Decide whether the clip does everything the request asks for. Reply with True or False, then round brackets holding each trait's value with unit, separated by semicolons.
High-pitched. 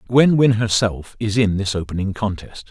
False (105 Hz)